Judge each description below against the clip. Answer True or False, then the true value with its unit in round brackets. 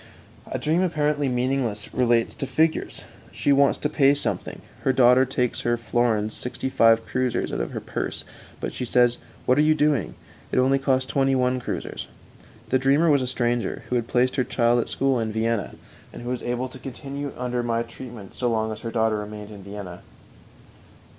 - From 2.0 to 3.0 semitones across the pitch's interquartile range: True (2.7 semitones)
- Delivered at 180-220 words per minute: True (195 wpm)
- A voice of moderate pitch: False (125 Hz)